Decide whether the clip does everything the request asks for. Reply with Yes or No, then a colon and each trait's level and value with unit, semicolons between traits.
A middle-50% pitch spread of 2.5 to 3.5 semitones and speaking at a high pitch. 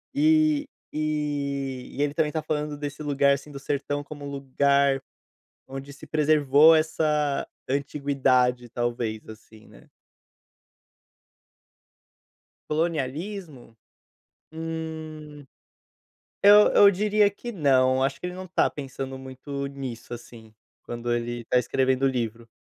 No: average, 2.9 semitones; medium, 140 Hz